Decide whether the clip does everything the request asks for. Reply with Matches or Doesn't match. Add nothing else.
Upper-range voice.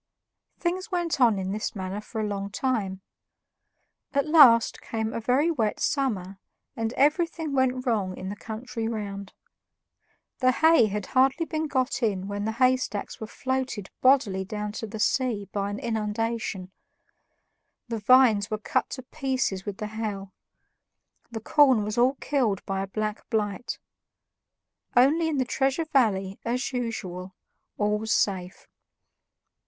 Matches